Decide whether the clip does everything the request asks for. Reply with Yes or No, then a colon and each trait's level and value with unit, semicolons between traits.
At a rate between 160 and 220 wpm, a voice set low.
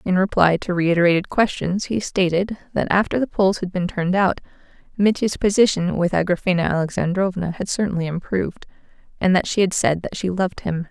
No: average, 175 wpm; medium, 185 Hz